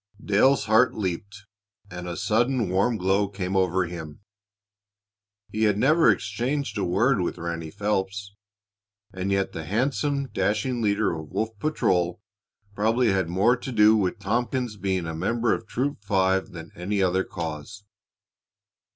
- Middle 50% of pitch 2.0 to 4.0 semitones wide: Yes, average, 3.7 semitones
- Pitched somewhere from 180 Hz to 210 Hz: No, low, 100 Hz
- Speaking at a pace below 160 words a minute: Yes, average, 145 wpm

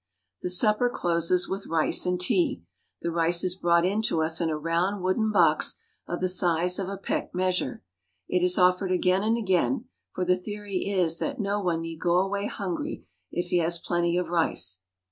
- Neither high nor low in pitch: Yes, medium, 180 Hz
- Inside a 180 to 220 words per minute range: Yes, average, 195 wpm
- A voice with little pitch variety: Yes, narrow, 2.3 semitones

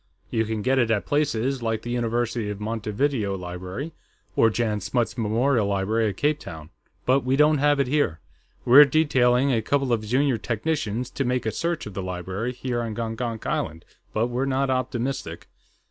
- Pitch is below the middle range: Yes, low, 120 Hz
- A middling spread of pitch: Yes, average, 3.9 semitones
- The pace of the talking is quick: No, average, 180 wpm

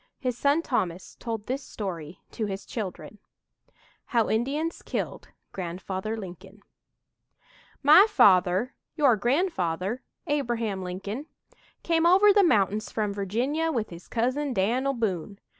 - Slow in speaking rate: Yes, slow, 120 wpm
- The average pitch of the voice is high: Yes, high, 225 Hz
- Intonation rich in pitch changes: Yes, wide, 6.3 semitones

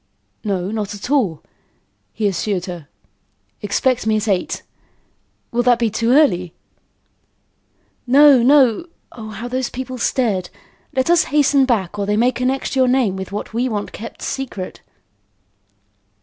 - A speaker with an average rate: Yes, average, 145 wpm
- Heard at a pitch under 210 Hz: No, high, 230 Hz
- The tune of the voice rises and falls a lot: No, average, 4.2 semitones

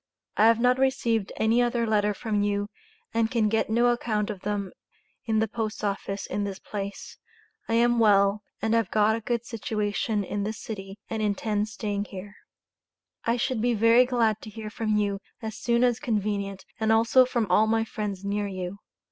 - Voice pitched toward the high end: Yes, high, 215 Hz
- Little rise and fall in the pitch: Yes, narrow, 2.0 semitones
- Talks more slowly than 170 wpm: No, average, 190 wpm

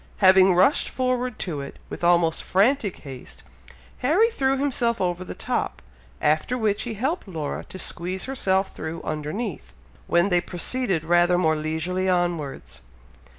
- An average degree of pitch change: No, wide, 5.9 semitones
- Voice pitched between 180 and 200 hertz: Yes, medium, 185 Hz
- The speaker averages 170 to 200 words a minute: No, average, 145 wpm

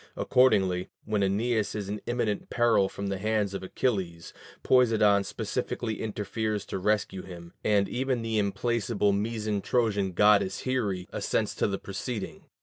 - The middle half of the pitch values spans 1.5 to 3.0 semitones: Yes, narrow, 2.6 semitones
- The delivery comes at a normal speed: Yes, average, 145 wpm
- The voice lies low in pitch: Yes, low, 105 Hz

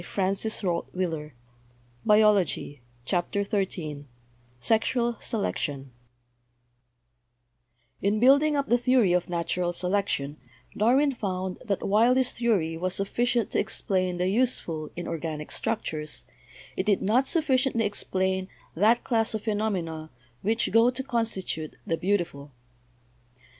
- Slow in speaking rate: Yes, slow, 110 wpm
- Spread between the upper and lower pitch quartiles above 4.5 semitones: Yes, wide, 5.4 semitones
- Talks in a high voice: Yes, high, 195 Hz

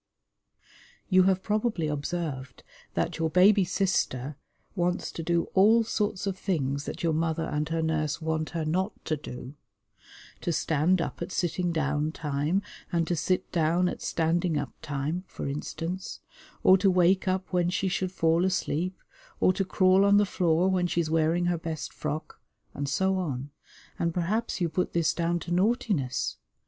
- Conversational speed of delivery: Yes, average, 170 wpm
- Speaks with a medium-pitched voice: Yes, medium, 170 Hz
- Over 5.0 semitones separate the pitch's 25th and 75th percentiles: No, average, 3.0 semitones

